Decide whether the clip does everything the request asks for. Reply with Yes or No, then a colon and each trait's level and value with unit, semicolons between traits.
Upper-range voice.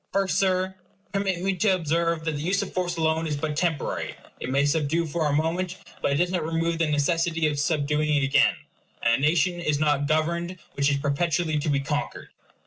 No: medium, 160 Hz